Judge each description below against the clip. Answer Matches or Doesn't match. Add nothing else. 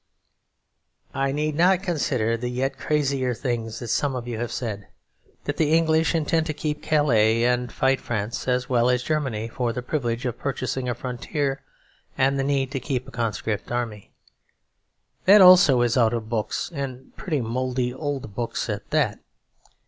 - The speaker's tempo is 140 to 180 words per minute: Matches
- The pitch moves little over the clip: Doesn't match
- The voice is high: Doesn't match